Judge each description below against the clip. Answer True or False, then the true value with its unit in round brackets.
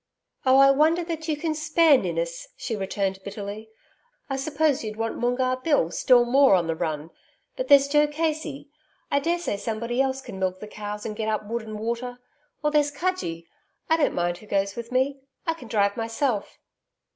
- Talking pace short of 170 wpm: False (190 wpm)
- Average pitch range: False (6.1 semitones)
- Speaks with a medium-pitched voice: False (250 Hz)